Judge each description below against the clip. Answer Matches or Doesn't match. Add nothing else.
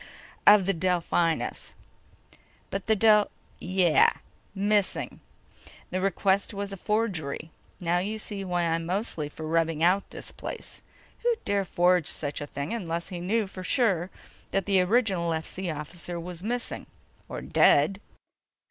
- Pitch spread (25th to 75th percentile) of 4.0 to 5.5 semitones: Doesn't match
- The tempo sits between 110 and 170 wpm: Matches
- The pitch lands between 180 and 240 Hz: Matches